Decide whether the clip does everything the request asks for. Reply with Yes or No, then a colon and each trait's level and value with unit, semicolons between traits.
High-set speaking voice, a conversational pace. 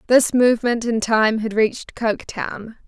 Yes: high, 225 Hz; average, 145 wpm